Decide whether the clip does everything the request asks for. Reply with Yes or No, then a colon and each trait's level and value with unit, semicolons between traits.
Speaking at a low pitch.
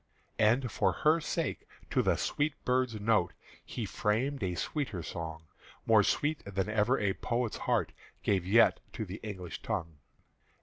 Yes: low, 110 Hz